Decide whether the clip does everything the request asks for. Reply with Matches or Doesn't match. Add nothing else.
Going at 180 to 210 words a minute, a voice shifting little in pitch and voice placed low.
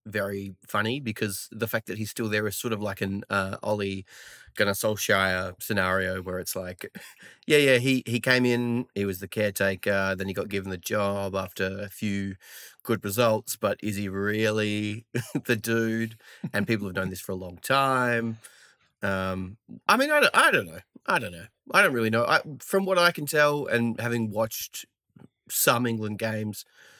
Doesn't match